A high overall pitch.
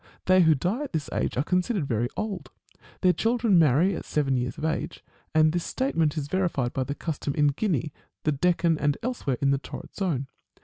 No: medium, 160 Hz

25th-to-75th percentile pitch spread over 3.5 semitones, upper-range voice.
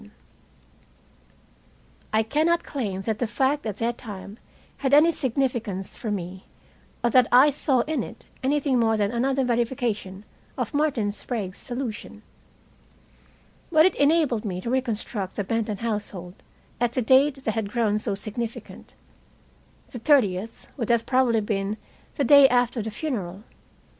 Yes: average, 4.1 semitones; high, 235 Hz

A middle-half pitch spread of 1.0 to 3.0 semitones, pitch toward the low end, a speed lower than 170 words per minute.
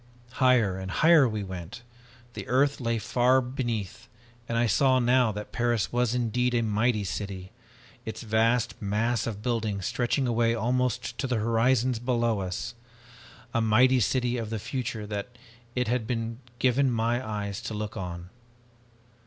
Yes: narrow, 2.6 semitones; low, 115 Hz; average, 155 wpm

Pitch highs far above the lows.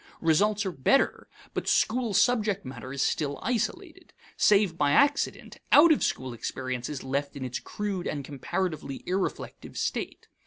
Yes: wide, 7.3 semitones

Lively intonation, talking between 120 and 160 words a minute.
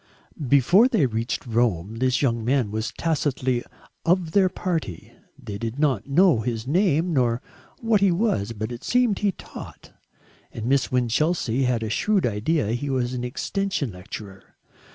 Yes: wide, 6.9 semitones; average, 155 wpm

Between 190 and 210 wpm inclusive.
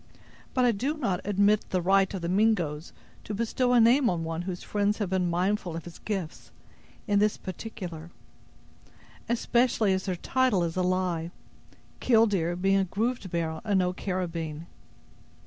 No: average, 165 wpm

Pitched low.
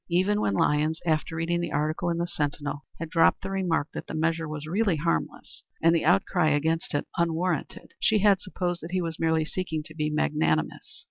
No: medium, 165 Hz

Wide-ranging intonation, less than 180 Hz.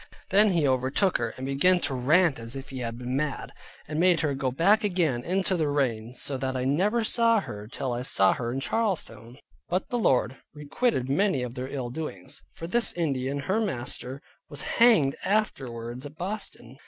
Yes: wide, 6.4 semitones; medium, 140 Hz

